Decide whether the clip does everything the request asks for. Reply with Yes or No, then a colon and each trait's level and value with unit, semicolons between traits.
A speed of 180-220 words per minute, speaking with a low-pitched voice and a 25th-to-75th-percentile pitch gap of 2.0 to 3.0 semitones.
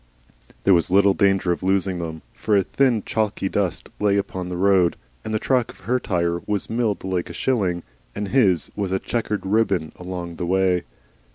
Yes: average, 190 wpm; very low, 95 Hz; average, 2.7 semitones